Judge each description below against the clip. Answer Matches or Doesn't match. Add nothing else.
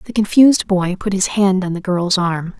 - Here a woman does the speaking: Matches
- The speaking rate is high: Matches